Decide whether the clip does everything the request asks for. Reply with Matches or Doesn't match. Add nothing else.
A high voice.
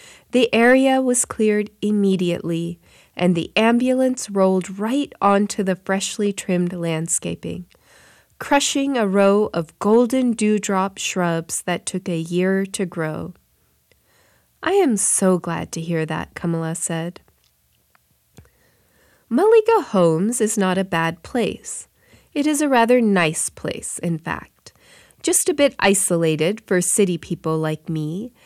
Matches